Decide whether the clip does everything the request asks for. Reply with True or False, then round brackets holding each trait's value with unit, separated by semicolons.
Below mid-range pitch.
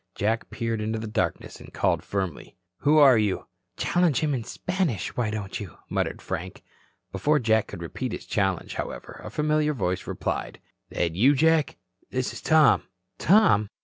True (115 Hz)